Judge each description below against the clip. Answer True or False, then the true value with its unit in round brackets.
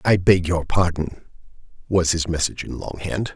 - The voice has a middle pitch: False (85 Hz)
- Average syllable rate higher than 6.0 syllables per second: False (5.0 syllables/s)